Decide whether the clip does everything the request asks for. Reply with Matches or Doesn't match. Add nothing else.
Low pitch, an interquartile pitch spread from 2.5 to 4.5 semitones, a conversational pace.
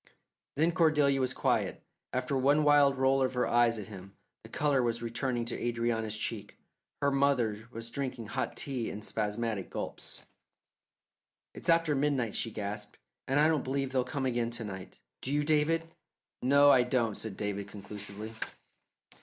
Matches